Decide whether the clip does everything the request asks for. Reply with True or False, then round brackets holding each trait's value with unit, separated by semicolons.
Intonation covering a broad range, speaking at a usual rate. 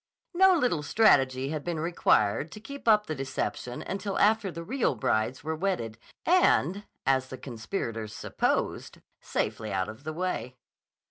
True (8.4 semitones; 150 wpm)